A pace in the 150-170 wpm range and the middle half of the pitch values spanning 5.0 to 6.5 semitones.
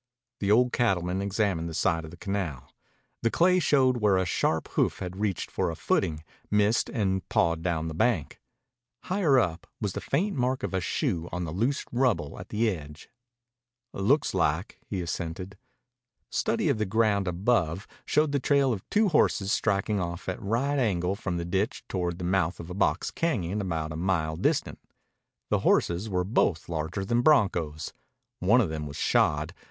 No: average, 180 wpm; average, 5.3 semitones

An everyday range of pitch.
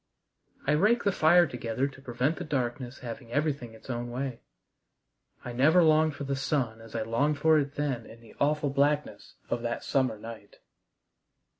Yes: average, 4.1 semitones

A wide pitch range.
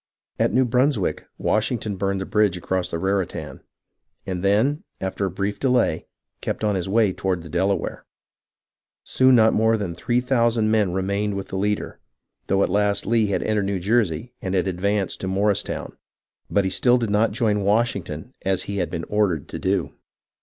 No: average, 2.8 semitones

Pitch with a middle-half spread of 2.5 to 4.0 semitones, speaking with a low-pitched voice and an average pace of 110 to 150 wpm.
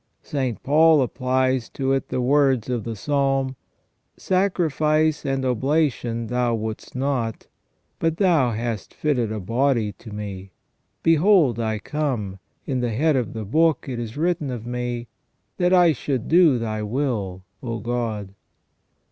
No: average, 4.5 semitones; low, 130 Hz; average, 145 wpm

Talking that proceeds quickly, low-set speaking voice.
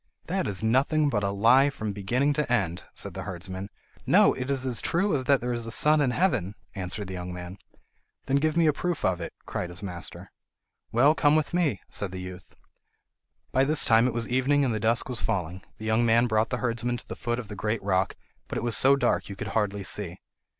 Yes: fast, 235 wpm; low, 115 Hz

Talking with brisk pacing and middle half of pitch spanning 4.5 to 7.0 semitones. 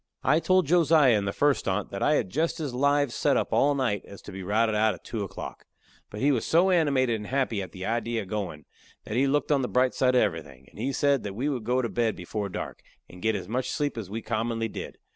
Yes: fast, 260 wpm; average, 5.2 semitones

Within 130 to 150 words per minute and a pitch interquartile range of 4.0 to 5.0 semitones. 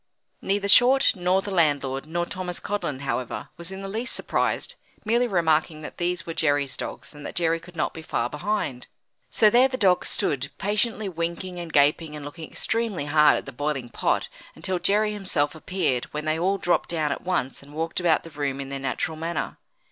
No: average, 200 wpm; average, 4.7 semitones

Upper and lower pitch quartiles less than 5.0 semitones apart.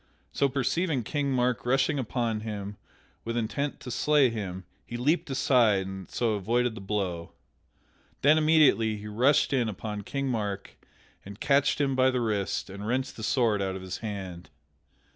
Yes: average, 4.6 semitones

